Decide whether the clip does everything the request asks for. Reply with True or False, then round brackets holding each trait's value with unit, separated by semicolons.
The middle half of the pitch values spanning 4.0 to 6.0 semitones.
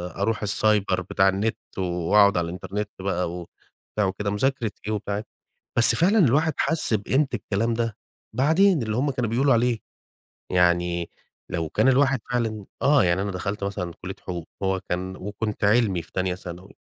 True (4.3 semitones)